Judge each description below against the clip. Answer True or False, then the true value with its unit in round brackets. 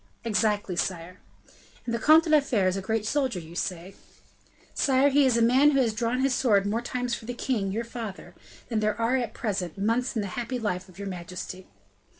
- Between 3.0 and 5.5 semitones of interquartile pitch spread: True (4.3 semitones)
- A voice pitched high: True (225 Hz)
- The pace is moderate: False (215 wpm)